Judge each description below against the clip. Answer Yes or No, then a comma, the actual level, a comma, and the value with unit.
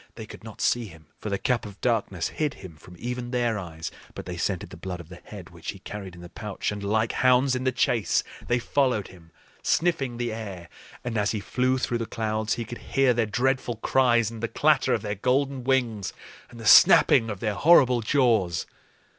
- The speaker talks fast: Yes, fast, 215 wpm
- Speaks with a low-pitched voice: Yes, low, 115 Hz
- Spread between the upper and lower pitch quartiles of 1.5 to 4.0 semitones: Yes, average, 3.7 semitones